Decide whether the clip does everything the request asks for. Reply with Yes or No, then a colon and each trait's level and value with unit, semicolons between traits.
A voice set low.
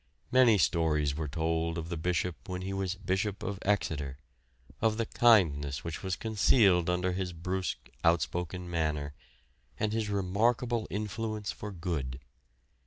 Yes: very low, 90 Hz